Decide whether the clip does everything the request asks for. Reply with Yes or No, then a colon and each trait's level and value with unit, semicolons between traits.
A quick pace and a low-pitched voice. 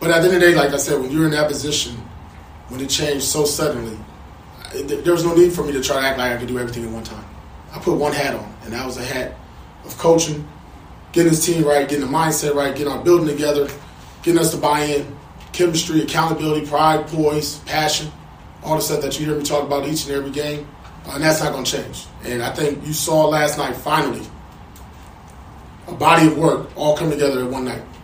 No: fast, 235 wpm; medium, 145 Hz